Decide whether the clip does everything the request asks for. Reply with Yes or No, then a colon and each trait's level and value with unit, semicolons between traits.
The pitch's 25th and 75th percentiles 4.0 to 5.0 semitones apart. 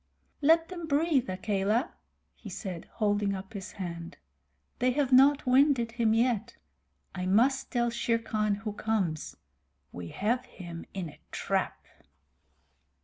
Yes: average, 4.7 semitones